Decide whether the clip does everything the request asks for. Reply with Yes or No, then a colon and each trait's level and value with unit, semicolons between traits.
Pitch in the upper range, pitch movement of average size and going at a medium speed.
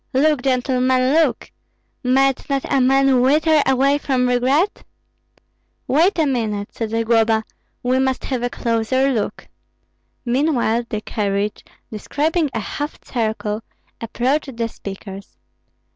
No: very high, 255 Hz; average, 3.2 semitones; slow, 120 wpm